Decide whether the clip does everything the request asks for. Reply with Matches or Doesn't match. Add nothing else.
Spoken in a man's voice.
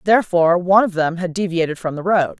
Doesn't match